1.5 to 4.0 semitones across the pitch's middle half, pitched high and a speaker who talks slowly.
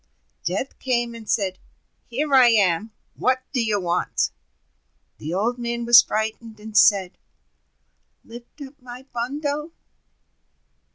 Yes: average, 3.3 semitones; high, 235 Hz; slow, 120 wpm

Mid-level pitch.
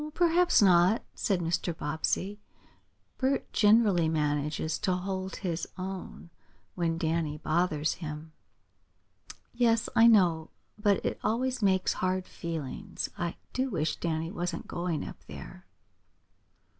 Yes: medium, 180 Hz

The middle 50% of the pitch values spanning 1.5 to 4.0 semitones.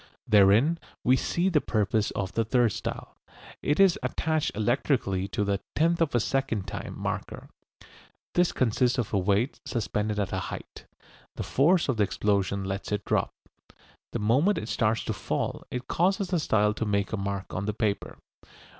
No: wide, 5.6 semitones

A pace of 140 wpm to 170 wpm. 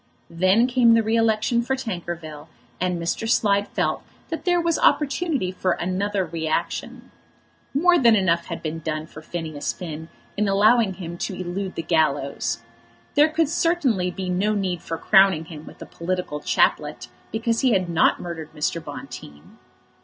Yes: average, 160 wpm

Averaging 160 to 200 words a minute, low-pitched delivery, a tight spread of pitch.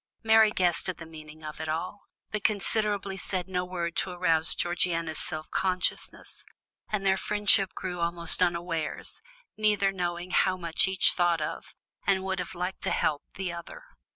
No: average, 165 wpm; medium, 180 Hz; narrow, 2.3 semitones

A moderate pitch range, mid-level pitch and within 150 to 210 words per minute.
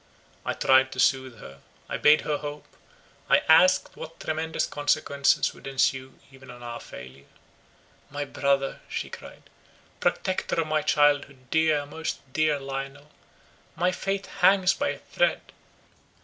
No: average, 3.0 semitones; medium, 145 Hz; average, 140 wpm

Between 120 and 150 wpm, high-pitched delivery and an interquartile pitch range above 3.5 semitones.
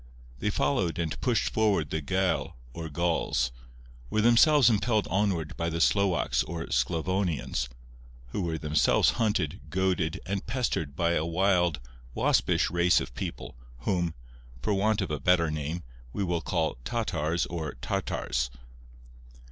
No: average, 140 wpm; very low, 85 Hz; average, 3.9 semitones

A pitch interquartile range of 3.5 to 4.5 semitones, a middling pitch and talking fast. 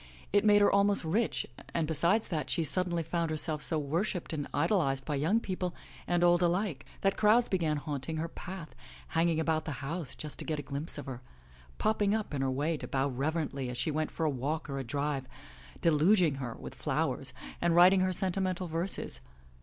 Yes: average, 4.1 semitones; medium, 160 Hz; fast, 215 wpm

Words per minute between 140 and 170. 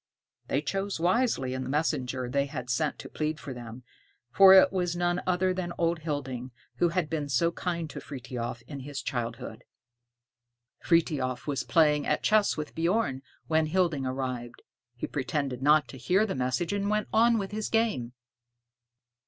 Yes: average, 165 wpm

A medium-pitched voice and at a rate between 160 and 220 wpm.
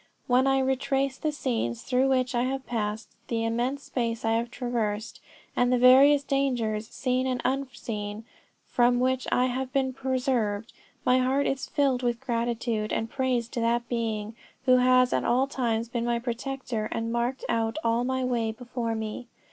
No: high, 245 Hz; average, 170 wpm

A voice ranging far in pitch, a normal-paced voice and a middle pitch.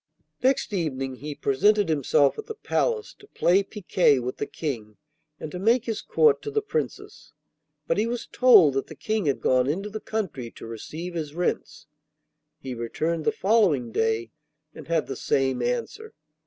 Yes: wide, 8.7 semitones; average, 175 wpm; medium, 170 Hz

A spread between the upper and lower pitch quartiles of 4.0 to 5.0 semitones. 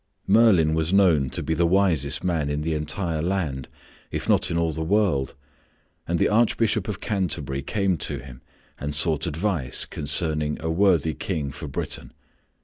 Yes: average, 4.5 semitones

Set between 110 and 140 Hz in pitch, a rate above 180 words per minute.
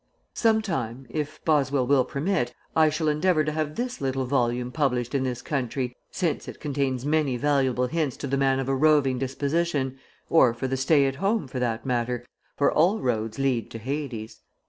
Yes: low, 135 Hz; average, 190 wpm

